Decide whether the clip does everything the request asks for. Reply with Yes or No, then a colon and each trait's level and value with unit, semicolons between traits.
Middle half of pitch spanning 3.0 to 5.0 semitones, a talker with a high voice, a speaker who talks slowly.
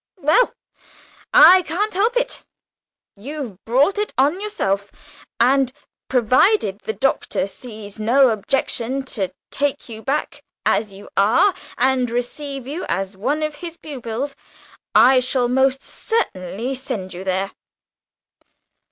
No: wide, 5.4 semitones; very high, 260 Hz; slow, 125 wpm